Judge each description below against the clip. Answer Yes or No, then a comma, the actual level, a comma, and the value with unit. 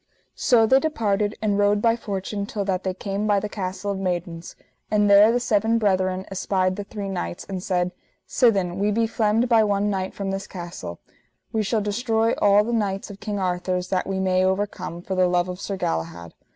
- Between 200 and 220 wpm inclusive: Yes, fast, 205 wpm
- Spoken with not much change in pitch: Yes, narrow, 2.2 semitones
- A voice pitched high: Yes, high, 200 Hz